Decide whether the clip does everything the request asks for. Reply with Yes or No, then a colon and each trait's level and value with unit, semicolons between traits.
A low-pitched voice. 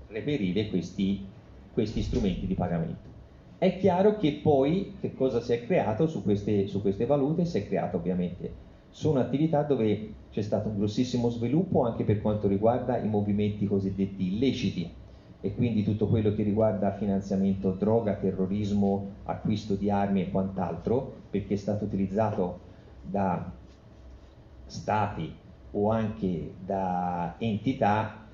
Yes: low, 105 Hz